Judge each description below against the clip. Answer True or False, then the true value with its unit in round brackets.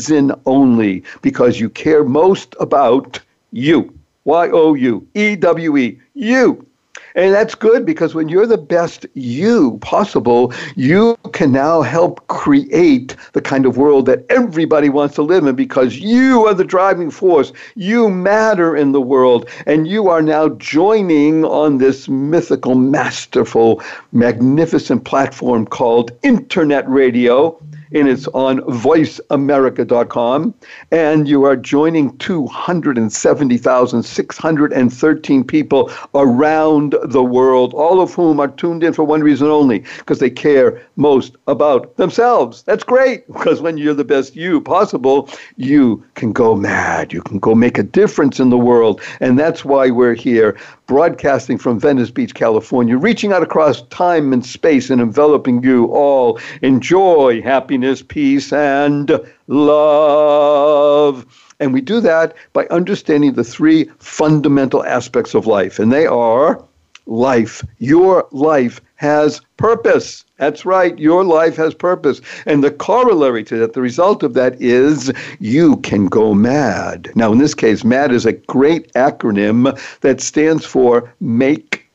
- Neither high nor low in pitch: True (150 Hz)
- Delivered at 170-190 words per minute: False (140 wpm)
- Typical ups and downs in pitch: True (4.9 semitones)